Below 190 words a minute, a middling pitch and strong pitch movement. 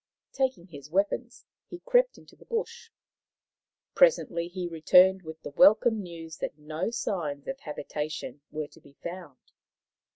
Yes: average, 140 wpm; medium, 175 Hz; wide, 7.6 semitones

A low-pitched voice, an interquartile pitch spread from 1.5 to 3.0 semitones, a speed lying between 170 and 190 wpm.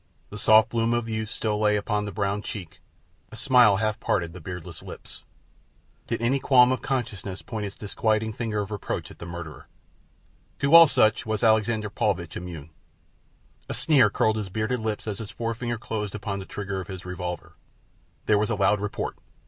Yes: low, 105 Hz; narrow, 2.4 semitones; average, 185 wpm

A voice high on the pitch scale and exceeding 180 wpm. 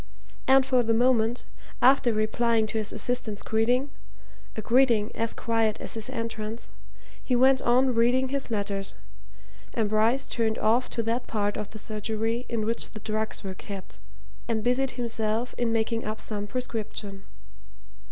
No: high, 225 Hz; average, 155 wpm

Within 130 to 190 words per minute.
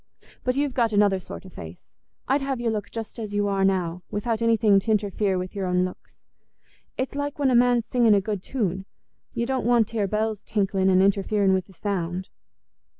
No: average, 200 wpm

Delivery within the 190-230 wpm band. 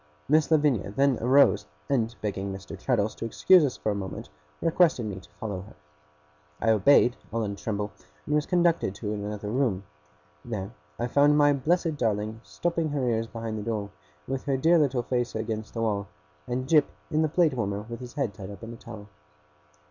Yes: average, 195 wpm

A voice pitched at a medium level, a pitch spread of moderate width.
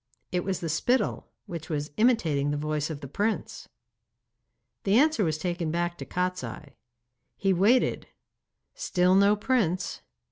Yes: medium, 180 Hz; average, 4.8 semitones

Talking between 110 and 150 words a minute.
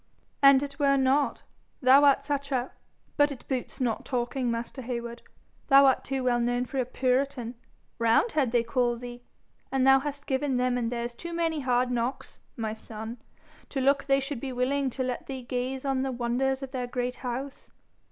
No: average, 190 wpm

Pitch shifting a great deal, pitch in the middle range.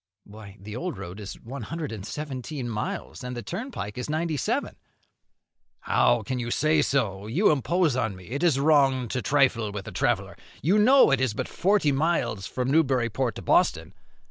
No: wide, 5.8 semitones; low, 130 Hz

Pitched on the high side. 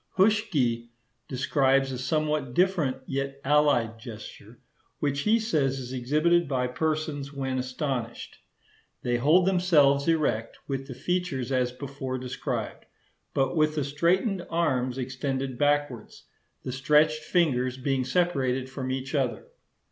No: low, 135 Hz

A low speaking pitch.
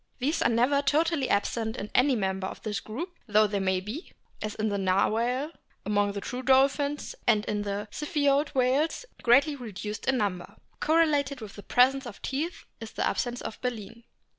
No: high, 240 Hz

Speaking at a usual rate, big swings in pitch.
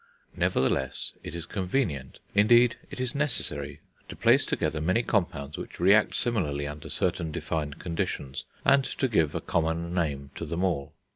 Yes: average, 155 wpm; wide, 6.3 semitones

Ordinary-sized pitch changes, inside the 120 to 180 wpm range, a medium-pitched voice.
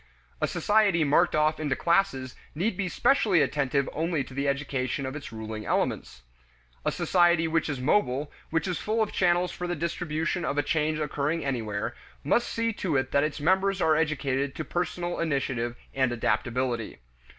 Yes: average, 4.4 semitones; average, 175 wpm; medium, 155 Hz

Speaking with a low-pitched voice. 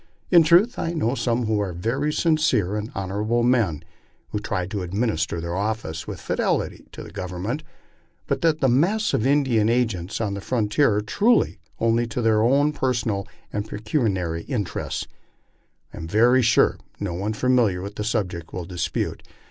Yes: low, 110 Hz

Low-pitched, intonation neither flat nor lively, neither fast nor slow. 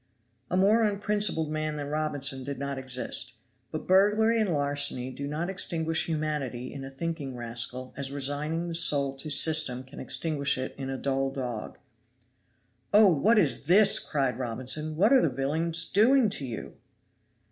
No: medium, 150 Hz; average, 4.1 semitones; average, 160 wpm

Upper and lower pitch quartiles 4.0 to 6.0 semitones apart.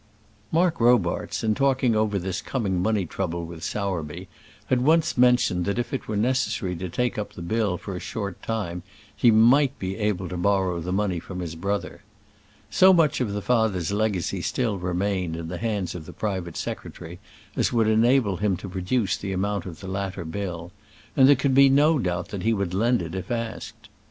Yes: average, 4.5 semitones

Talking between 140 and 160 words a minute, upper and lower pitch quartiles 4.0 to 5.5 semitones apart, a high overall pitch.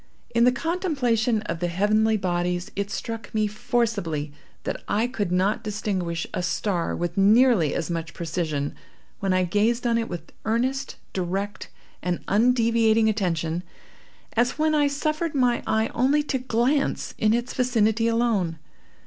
Yes: average, 150 wpm; average, 5.1 semitones; high, 220 Hz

